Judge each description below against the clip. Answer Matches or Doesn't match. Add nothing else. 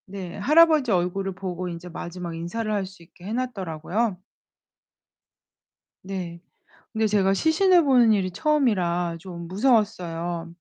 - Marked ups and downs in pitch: Doesn't match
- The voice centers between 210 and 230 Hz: Doesn't match